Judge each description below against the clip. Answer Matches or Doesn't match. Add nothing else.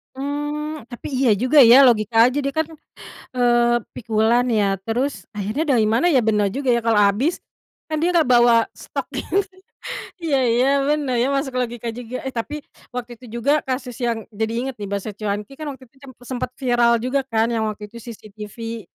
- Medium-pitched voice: Doesn't match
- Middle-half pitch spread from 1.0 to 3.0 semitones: Doesn't match